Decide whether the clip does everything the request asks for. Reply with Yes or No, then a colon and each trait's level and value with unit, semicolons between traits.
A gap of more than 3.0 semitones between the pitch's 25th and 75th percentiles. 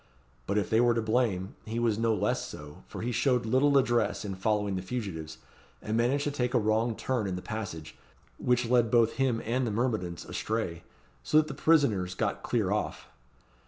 Yes: average, 3.6 semitones